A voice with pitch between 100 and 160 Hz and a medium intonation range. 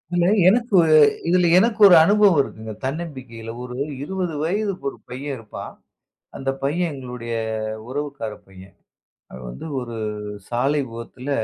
No: medium, 140 Hz; wide, 6.9 semitones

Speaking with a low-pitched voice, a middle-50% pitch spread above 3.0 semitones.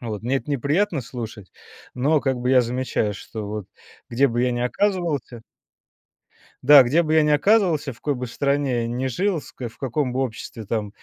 Yes: low, 130 Hz; average, 3.9 semitones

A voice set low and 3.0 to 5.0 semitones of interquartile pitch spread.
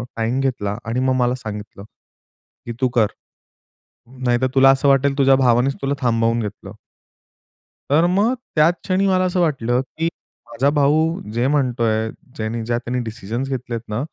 Yes: low, 125 Hz; average, 3.5 semitones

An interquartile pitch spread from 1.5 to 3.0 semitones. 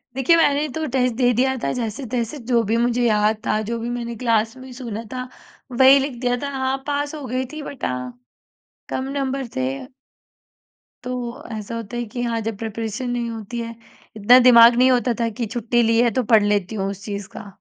Yes: narrow, 2.5 semitones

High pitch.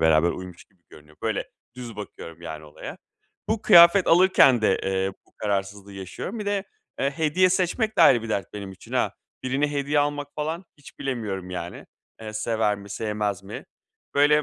No: low, 110 Hz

